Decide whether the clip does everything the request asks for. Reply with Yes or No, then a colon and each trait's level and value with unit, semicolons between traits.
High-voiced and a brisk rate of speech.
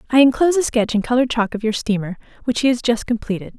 Yes: high, 235 Hz; fast, 250 wpm